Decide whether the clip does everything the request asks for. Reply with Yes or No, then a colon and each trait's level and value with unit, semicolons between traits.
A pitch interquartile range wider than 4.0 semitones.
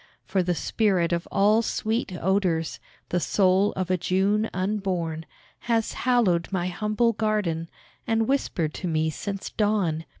No: average, 3.7 semitones